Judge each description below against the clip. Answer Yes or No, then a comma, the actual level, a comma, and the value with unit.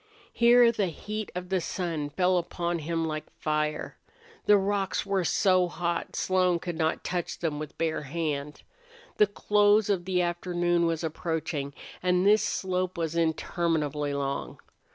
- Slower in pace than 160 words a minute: Yes, average, 150 wpm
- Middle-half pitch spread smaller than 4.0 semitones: Yes, average, 2.9 semitones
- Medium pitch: Yes, medium, 175 Hz